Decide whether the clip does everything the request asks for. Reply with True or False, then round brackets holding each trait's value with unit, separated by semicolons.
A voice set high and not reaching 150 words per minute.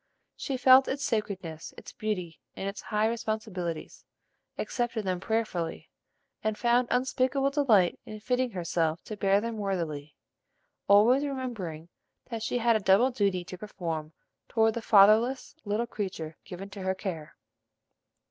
True (210 Hz; 140 wpm)